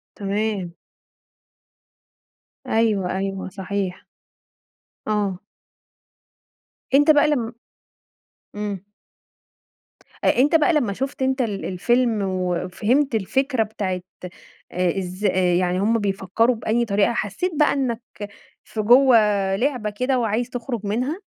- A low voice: No, high, 215 Hz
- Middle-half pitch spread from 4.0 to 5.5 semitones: Yes, average, 4.5 semitones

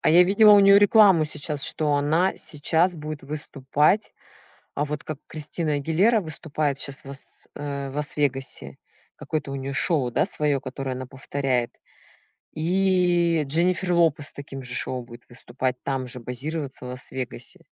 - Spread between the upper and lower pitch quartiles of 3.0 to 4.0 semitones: Yes, average, 3.7 semitones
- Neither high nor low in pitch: Yes, medium, 145 Hz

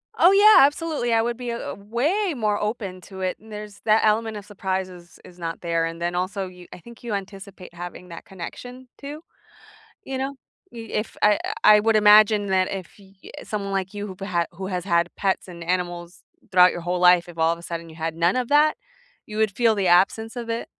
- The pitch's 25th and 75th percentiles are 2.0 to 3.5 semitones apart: No, average, 4.0 semitones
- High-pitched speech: Yes, high, 200 Hz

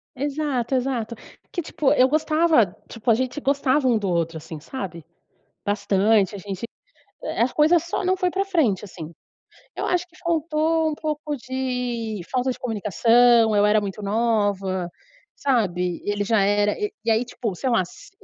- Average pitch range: No, wide, 6.4 semitones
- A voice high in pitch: Yes, high, 235 Hz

